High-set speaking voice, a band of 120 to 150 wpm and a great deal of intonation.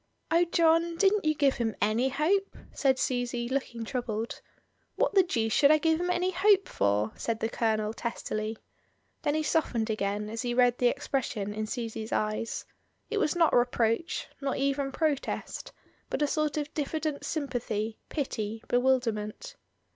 No: very high, 255 Hz; average, 160 wpm; wide, 5.7 semitones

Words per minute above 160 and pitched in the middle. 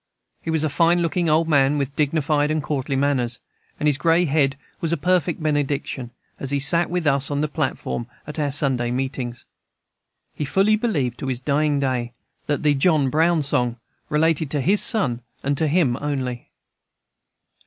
Yes: average, 175 wpm; medium, 145 Hz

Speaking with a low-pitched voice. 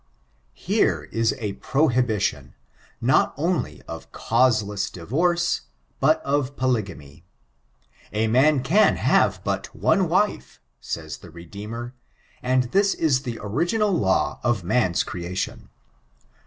Yes: low, 125 Hz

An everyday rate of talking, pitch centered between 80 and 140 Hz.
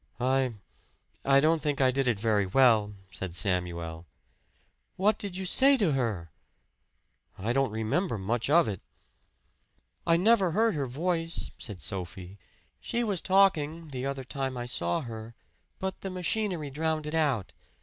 Yes: average, 150 wpm; low, 135 Hz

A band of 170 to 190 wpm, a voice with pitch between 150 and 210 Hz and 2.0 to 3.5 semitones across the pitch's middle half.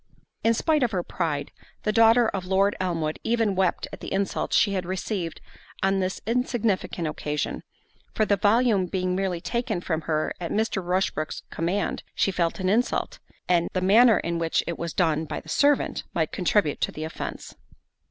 No: average, 180 wpm; high, 190 Hz; average, 4.1 semitones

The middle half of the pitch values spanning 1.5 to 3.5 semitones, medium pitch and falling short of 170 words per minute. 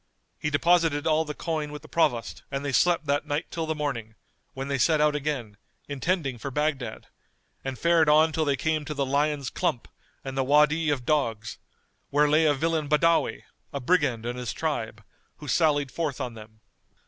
No: average, 2.9 semitones; medium, 145 Hz; average, 190 wpm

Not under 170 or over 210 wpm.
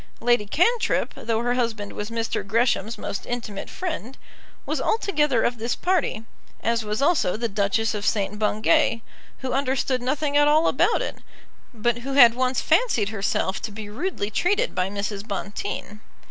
No: average, 160 wpm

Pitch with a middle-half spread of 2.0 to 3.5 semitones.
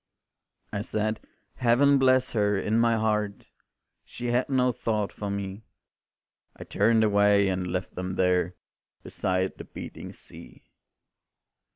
Yes: average, 3.2 semitones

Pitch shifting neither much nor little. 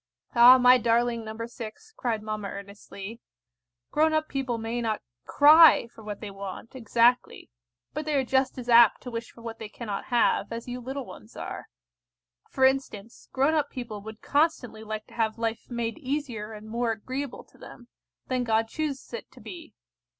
Yes: average, 3.2 semitones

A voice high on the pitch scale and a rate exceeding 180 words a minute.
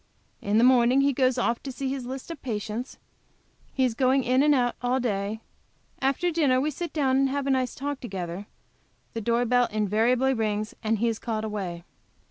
Yes: very high, 250 Hz; average, 200 wpm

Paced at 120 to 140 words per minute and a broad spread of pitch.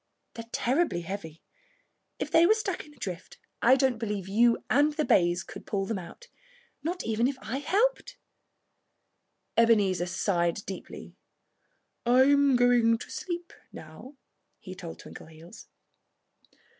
Yes: slow, 135 wpm; wide, 7.2 semitones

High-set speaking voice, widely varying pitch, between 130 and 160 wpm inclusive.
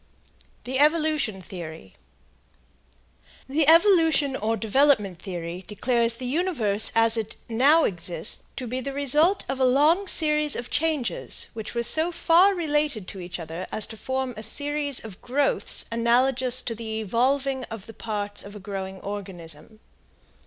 Yes: high, 245 Hz; wide, 5.9 semitones; average, 150 wpm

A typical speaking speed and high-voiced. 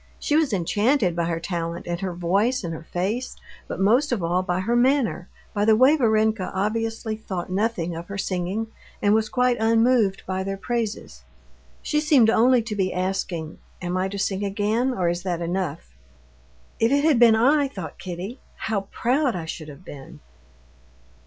Yes: average, 180 wpm; high, 205 Hz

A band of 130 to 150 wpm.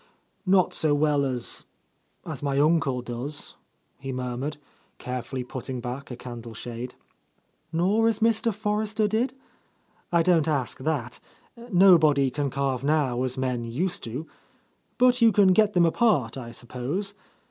Yes: average, 145 wpm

